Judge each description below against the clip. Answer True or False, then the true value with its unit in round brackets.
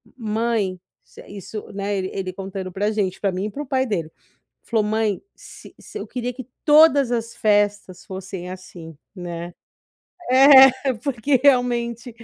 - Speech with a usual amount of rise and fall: True (4.6 semitones)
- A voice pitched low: False (215 Hz)